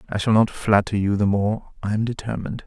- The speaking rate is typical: No, fast, 225 wpm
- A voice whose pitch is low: Yes, low, 105 Hz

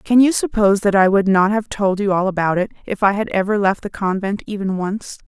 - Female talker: Yes, female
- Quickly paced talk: Yes, fast, 250 wpm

